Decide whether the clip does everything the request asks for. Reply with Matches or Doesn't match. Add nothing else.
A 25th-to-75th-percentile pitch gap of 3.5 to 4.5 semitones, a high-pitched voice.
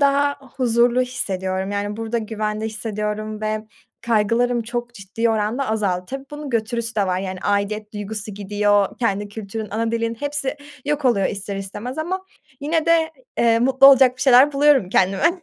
Matches